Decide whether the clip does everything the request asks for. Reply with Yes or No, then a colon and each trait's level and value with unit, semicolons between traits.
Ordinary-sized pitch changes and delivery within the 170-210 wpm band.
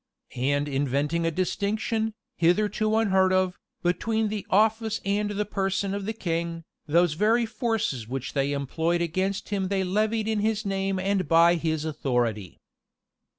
No: average, 4.3 semitones; average, 150 wpm